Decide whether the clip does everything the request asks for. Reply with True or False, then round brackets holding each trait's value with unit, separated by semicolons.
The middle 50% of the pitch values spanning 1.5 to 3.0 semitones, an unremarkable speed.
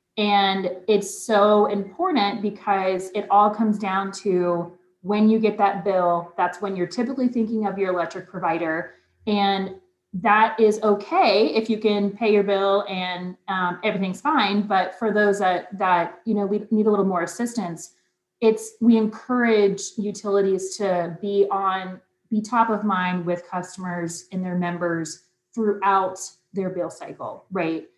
True (2.6 semitones; 155 wpm)